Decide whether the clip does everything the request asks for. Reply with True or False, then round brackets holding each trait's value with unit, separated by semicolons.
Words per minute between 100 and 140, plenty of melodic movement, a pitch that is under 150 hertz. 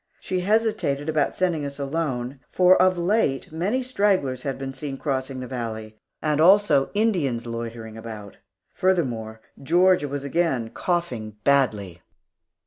True (135 wpm; 6.6 semitones; 140 Hz)